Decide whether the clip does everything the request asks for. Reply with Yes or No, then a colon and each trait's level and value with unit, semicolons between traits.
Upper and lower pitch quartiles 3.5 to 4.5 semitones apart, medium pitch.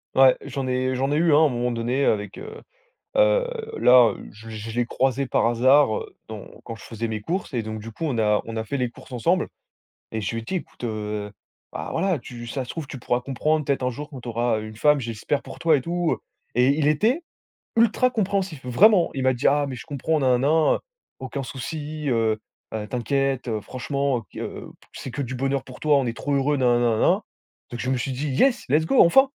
No: average, 4.2 semitones; low, 130 Hz